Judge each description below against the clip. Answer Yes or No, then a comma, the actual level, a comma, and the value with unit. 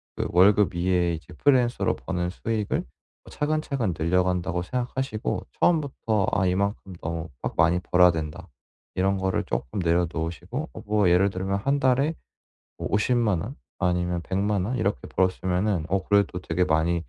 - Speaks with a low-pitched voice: Yes, very low, 95 Hz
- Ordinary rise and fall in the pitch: Yes, average, 3.6 semitones